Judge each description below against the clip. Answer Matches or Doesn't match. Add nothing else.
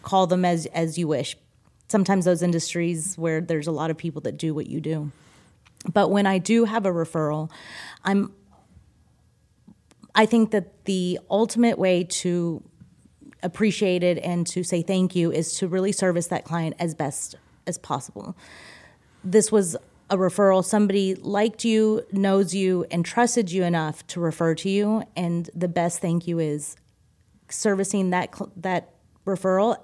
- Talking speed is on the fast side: Doesn't match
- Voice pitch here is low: Doesn't match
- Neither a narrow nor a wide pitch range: Matches